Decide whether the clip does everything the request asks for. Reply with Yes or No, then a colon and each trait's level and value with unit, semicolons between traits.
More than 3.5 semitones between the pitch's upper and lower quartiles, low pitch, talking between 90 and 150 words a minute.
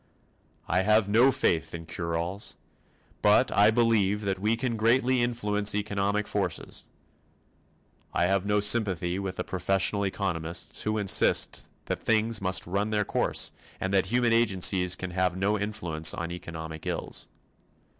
No: average, 2.9 semitones; low, 100 Hz; average, 145 wpm